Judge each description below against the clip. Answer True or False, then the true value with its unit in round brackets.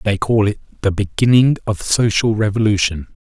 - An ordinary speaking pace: True (150 wpm)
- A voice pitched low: True (105 Hz)